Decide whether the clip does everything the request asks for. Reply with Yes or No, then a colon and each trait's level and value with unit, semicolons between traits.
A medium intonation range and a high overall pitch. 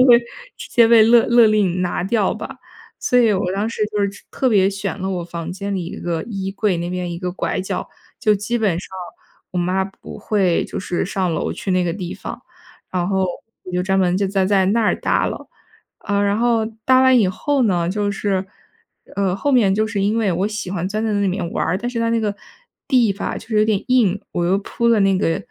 Yes: average, 3.0 semitones; high, 200 Hz